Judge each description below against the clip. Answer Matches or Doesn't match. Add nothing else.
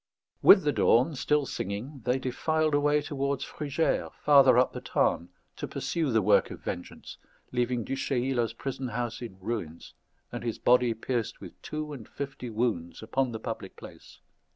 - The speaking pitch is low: Matches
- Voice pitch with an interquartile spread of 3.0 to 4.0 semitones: Matches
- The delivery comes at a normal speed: Matches